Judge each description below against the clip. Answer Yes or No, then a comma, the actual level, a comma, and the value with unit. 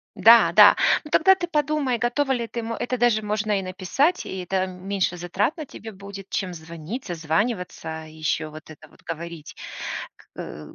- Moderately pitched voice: No, high, 195 Hz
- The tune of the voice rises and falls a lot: Yes, wide, 6.1 semitones